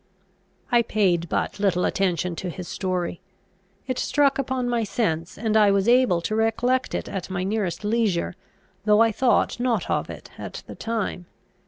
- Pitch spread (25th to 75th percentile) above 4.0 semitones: Yes, average, 4.5 semitones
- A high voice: Yes, high, 210 Hz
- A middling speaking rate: Yes, average, 170 wpm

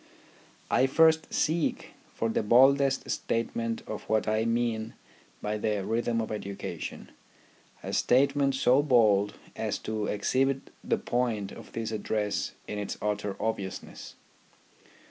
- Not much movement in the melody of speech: No, average, 3.8 semitones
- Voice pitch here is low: Yes, low, 115 Hz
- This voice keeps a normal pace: No, slow, 125 wpm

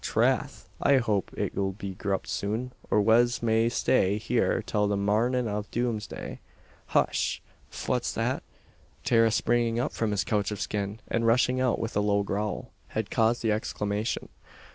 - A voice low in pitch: Yes, low, 110 Hz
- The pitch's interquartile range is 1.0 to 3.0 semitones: Yes, narrow, 2.4 semitones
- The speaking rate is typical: Yes, average, 160 wpm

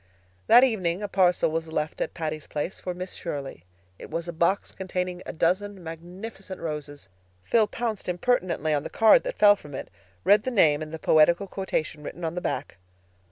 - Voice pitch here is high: No, medium, 175 Hz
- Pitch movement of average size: Yes, average, 3.8 semitones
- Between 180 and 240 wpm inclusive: Yes, average, 190 wpm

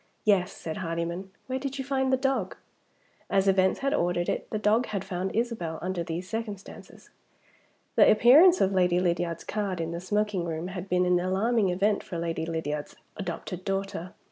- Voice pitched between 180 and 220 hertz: Yes, high, 190 Hz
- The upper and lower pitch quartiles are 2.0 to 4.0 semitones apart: Yes, average, 3.6 semitones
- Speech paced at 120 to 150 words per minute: No, average, 175 wpm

